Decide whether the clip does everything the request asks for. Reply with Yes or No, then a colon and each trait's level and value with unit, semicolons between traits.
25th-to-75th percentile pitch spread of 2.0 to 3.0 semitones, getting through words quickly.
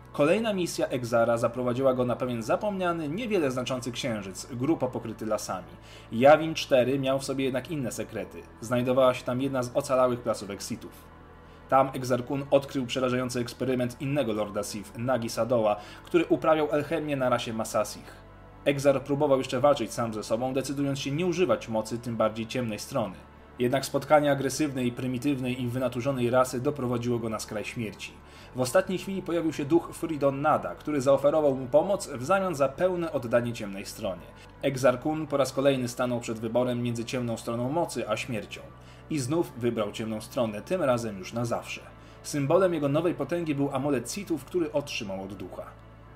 No: average, 4.0 semitones; fast, 165 wpm